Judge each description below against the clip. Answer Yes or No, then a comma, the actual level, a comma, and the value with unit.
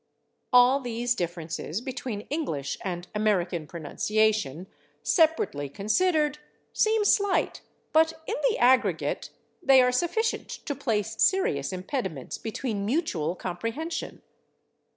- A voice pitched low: No, high, 230 Hz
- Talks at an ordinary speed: No, slow, 110 wpm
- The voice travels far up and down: Yes, wide, 8.7 semitones